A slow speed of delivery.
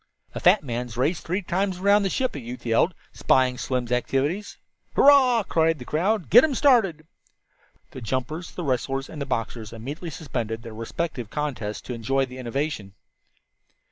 No: average, 165 wpm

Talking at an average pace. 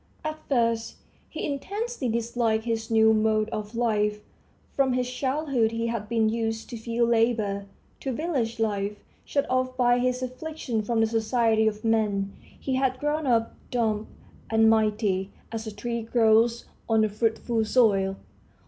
Yes: average, 155 wpm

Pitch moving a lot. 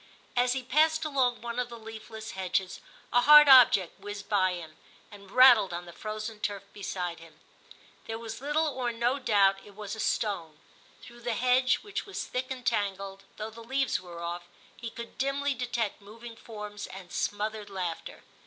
No: average, 4.1 semitones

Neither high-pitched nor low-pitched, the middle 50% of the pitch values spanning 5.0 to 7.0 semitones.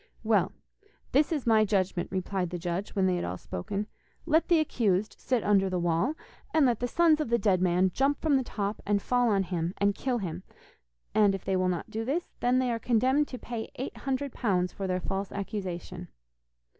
No: high, 205 Hz; wide, 5.4 semitones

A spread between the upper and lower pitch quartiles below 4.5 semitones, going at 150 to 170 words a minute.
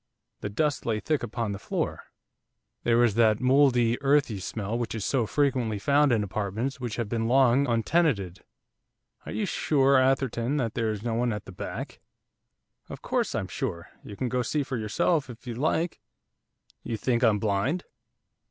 No: average, 3.8 semitones; average, 180 wpm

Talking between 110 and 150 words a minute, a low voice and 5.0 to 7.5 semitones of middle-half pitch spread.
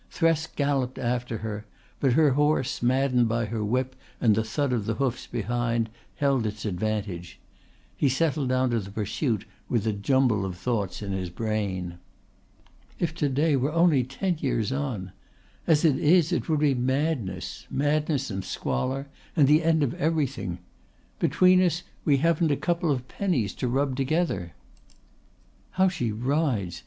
No: average, 160 wpm; low, 130 Hz; wide, 5.4 semitones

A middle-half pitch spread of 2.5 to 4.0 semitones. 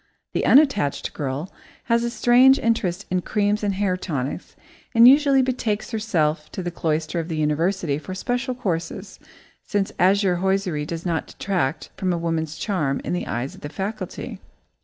No: average, 5.1 semitones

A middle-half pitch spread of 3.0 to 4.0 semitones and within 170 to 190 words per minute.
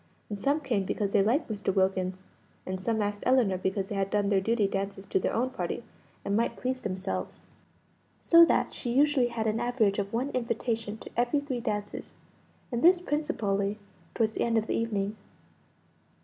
Yes: average, 3.6 semitones; average, 185 wpm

